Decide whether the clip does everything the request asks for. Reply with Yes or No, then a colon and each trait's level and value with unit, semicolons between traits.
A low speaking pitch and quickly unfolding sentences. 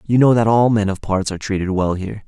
Yes: low, 105 Hz; fast, 290 wpm